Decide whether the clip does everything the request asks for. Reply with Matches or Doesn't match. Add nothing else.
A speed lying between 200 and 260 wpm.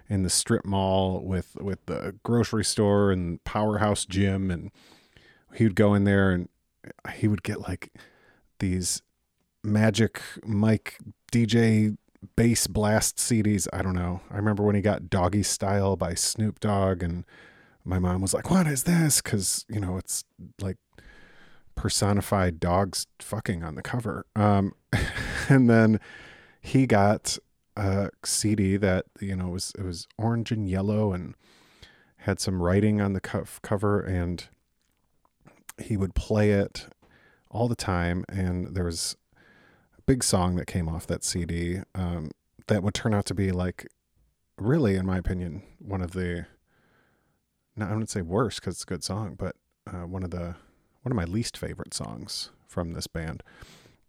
Doesn't match